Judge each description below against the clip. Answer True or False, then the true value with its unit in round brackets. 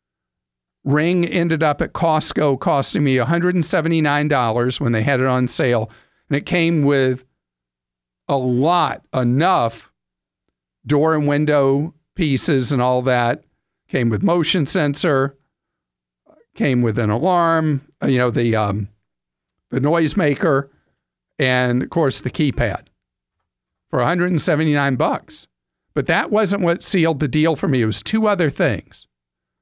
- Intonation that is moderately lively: False (6.2 semitones)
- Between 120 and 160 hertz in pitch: True (135 Hz)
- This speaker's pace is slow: True (130 wpm)